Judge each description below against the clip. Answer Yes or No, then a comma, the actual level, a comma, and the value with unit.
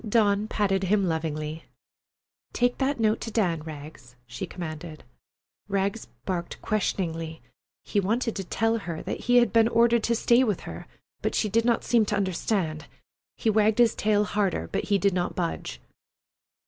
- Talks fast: No, average, 165 wpm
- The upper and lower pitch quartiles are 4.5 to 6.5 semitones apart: Yes, average, 5.2 semitones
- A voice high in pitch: Yes, high, 200 Hz